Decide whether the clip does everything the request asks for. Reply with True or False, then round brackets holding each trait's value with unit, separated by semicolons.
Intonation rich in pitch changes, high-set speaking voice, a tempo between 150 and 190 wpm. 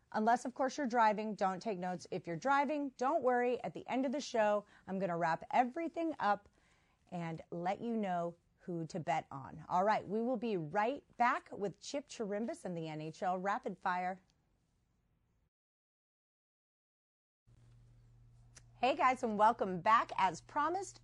True (6.4 semitones; 195 Hz; 155 wpm)